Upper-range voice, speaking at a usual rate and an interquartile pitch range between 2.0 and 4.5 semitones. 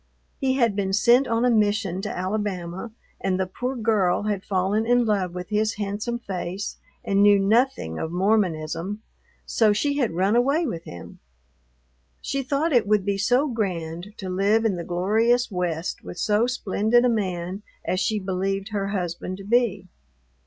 Yes: high, 205 Hz; average, 170 wpm; average, 3.7 semitones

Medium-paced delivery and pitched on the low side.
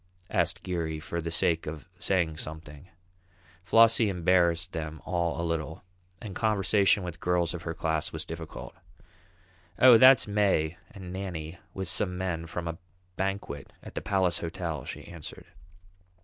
Yes: average, 150 wpm; very low, 85 Hz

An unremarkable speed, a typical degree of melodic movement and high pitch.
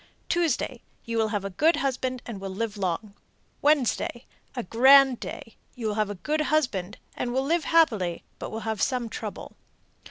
Yes: average, 180 wpm; average, 4.7 semitones; high, 235 Hz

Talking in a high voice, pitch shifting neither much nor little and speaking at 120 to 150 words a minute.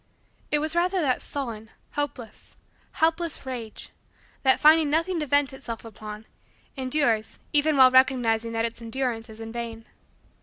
Yes: very high, 260 Hz; average, 4.7 semitones; average, 145 wpm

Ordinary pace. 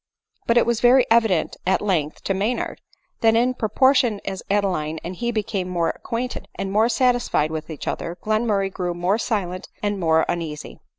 Yes: average, 175 wpm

